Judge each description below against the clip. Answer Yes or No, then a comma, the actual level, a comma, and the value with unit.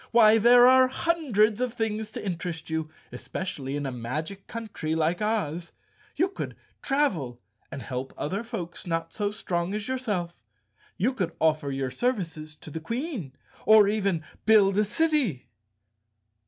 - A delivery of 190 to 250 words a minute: No, average, 150 wpm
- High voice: Yes, high, 195 Hz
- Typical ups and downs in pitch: No, wide, 6.4 semitones